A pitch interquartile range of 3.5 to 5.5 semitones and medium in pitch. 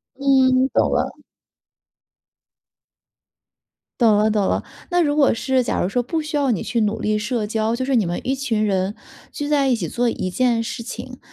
No: average, 4.0 semitones; high, 240 Hz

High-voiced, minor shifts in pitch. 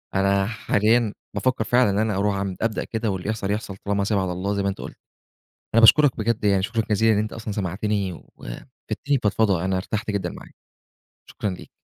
No: low, 105 Hz; narrow, 2.2 semitones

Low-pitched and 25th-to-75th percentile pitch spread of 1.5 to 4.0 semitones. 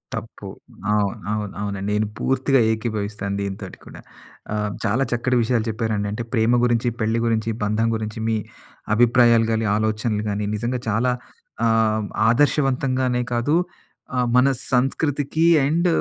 Yes: low, 115 Hz; average, 2.8 semitones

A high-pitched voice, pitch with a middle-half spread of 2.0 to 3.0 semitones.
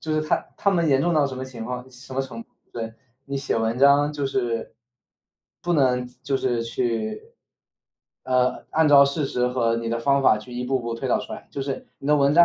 No: low, 130 Hz; average, 2.7 semitones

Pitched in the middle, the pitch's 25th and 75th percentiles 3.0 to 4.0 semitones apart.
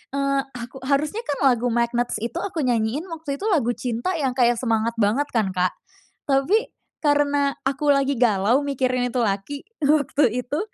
No: very high, 260 Hz; average, 3.3 semitones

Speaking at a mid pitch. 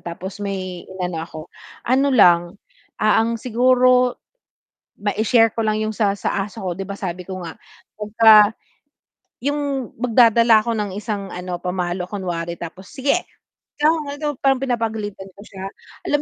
No: high, 210 Hz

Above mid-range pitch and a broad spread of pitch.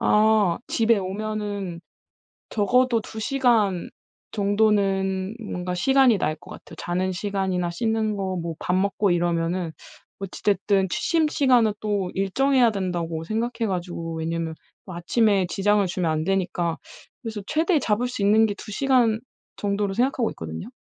No: high, 200 Hz; average, 3.7 semitones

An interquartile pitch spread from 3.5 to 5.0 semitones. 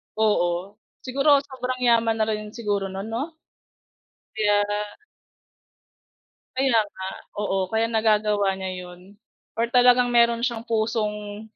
No: narrow, 2.5 semitones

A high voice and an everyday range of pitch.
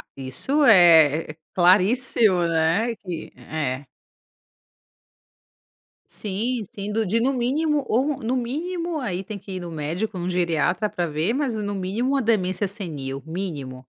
No: high, 195 Hz; wide, 6.0 semitones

